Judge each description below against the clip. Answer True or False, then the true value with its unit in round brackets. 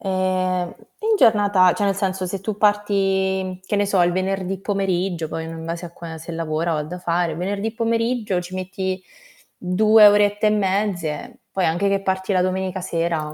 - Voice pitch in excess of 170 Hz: True (190 Hz)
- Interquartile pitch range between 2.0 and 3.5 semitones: True (2.4 semitones)